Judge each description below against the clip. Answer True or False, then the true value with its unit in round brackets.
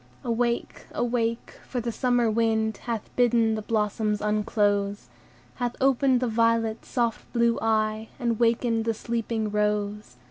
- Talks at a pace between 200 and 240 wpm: False (135 wpm)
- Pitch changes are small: True (1.6 semitones)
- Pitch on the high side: True (225 Hz)